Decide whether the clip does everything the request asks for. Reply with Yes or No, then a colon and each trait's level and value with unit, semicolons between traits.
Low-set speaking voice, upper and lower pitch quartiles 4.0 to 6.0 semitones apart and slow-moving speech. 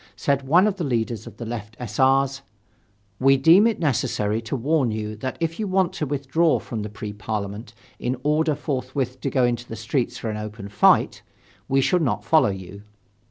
No: low, 130 Hz; average, 5.2 semitones; average, 200 wpm